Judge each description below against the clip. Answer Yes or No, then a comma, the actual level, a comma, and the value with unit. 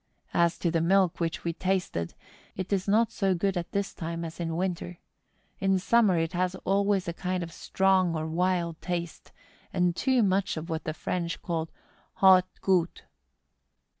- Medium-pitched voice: Yes, medium, 180 Hz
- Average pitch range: No, narrow, 2.3 semitones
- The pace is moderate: Yes, average, 170 wpm